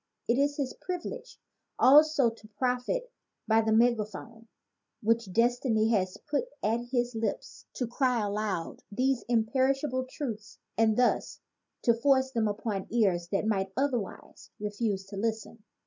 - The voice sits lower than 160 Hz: No, high, 230 Hz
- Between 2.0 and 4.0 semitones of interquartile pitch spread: Yes, average, 3.4 semitones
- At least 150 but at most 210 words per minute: No, average, 140 wpm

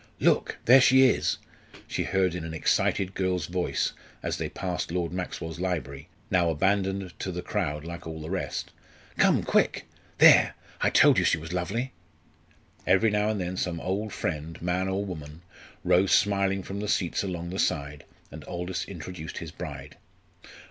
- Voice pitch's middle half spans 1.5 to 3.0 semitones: Yes, average, 2.7 semitones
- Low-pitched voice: Yes, very low, 90 Hz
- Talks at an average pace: Yes, average, 170 wpm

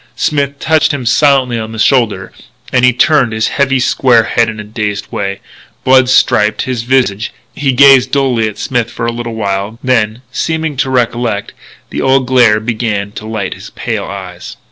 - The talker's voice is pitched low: Yes, low, 120 Hz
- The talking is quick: No, average, 180 wpm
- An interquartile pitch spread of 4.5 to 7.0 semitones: No, average, 3.4 semitones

